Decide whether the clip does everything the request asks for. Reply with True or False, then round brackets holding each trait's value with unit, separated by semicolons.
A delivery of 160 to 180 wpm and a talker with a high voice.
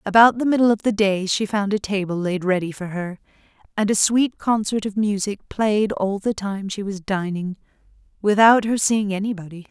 False (190 wpm; 205 Hz)